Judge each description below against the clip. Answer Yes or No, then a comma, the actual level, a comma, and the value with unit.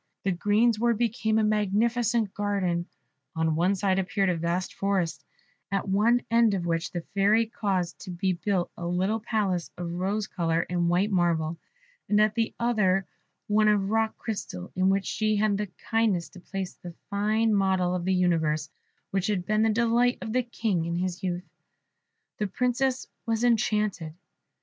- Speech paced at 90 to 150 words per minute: No, average, 170 wpm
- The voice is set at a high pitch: Yes, high, 200 Hz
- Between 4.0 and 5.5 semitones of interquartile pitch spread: No, average, 3.5 semitones